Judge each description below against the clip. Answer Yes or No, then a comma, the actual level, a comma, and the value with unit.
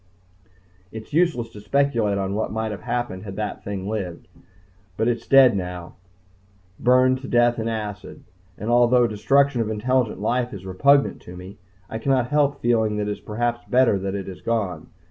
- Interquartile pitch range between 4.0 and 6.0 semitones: No, average, 3.5 semitones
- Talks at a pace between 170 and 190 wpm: Yes, average, 185 wpm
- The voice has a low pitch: Yes, low, 110 Hz